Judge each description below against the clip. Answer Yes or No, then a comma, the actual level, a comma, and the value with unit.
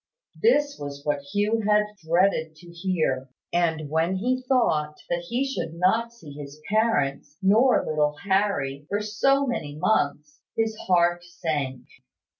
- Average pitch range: No, wide, 6.4 semitones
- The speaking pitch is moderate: Yes, medium, 175 Hz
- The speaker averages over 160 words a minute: No, average, 140 wpm